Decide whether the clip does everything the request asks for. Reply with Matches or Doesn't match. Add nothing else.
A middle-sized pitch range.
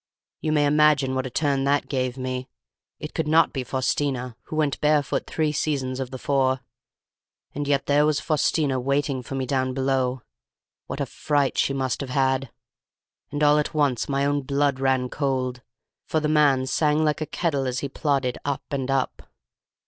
Doesn't match